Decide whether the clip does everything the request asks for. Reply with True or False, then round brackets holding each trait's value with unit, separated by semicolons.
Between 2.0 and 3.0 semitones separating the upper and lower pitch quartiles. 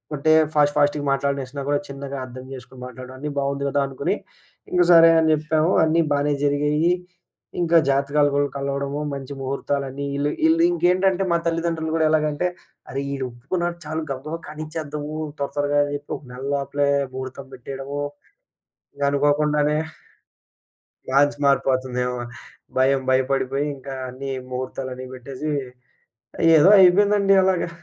True (2.4 semitones)